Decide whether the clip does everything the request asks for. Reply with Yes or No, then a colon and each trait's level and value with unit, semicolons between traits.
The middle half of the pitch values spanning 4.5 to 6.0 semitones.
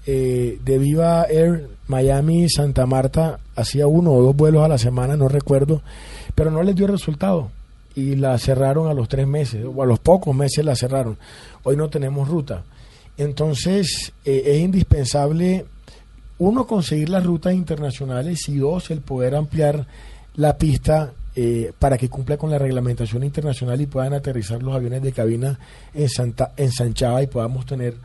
No: average, 3.5 semitones